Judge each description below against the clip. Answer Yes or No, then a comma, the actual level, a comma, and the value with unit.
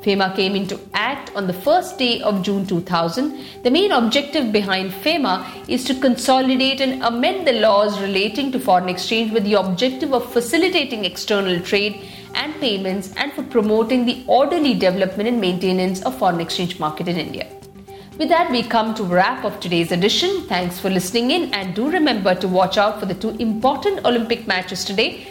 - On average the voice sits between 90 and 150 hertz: No, high, 210 Hz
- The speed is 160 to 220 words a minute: Yes, average, 180 wpm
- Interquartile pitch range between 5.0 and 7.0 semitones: Yes, wide, 5.5 semitones